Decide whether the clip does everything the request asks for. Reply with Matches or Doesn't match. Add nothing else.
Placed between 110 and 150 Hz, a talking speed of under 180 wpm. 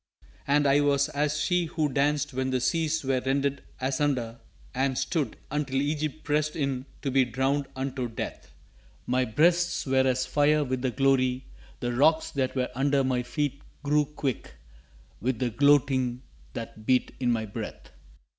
Matches